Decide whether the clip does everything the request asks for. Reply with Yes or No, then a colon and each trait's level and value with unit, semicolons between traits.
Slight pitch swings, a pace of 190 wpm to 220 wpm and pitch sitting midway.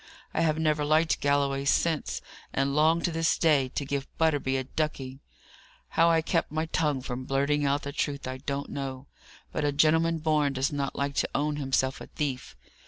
Yes: narrow, 2.3 semitones; average, 195 wpm; medium, 145 Hz